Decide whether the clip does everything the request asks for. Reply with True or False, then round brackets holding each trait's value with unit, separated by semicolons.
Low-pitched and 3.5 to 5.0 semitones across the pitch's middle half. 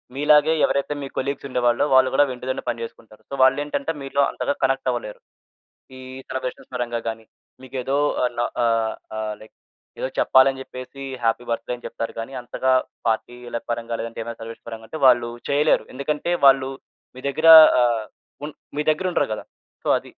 False (130 Hz; 2.9 semitones)